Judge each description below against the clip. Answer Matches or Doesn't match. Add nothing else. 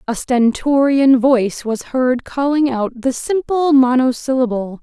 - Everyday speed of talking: Doesn't match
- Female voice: Matches